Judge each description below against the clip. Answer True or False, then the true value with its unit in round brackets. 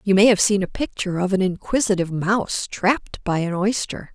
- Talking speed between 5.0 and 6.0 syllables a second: True (5.7 syllables/s)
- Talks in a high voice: True (195 Hz)